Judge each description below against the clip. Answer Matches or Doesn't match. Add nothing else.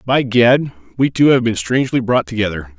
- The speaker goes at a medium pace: Matches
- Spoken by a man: Matches